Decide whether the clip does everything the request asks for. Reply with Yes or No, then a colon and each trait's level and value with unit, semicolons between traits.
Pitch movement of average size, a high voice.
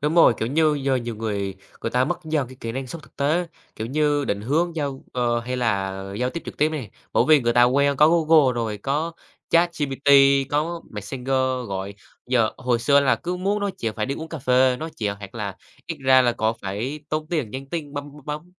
No: average, 4.7 semitones; low, 135 Hz